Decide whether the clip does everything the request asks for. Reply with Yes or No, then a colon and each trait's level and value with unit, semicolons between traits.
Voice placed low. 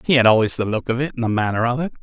Yes: low, 120 Hz